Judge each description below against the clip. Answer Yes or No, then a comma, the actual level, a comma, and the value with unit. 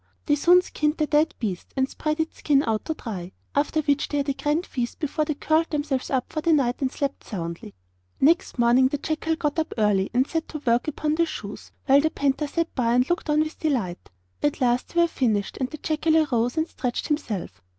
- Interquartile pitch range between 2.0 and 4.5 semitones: Yes, average, 4.2 semitones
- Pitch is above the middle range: Yes, very high, 285 Hz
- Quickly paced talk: Yes, fast, 225 wpm